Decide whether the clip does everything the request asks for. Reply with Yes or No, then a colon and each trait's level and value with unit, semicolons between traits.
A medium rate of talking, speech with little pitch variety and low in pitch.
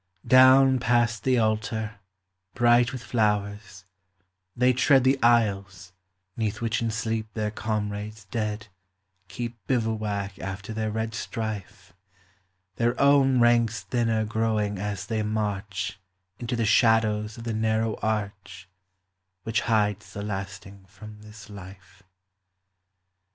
No: slow, 120 wpm; narrow, 2.2 semitones; low, 110 Hz